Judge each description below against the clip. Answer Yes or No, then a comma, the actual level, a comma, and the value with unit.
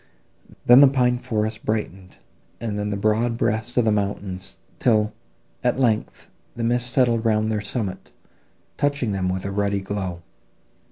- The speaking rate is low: No, average, 155 wpm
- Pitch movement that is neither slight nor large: Yes, average, 3.1 semitones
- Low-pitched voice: Yes, low, 110 Hz